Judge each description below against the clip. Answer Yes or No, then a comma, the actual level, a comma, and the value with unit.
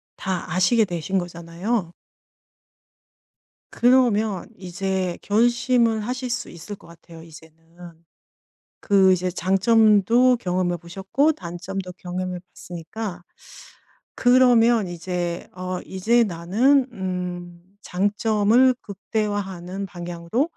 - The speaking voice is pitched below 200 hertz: Yes, high, 190 Hz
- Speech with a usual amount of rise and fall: Yes, average, 4.3 semitones